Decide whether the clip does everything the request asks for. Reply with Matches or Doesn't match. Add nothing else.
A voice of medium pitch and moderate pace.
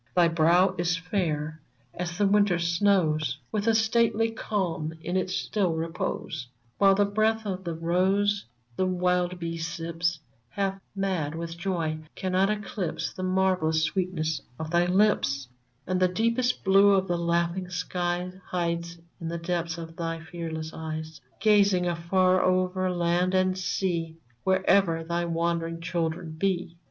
Matches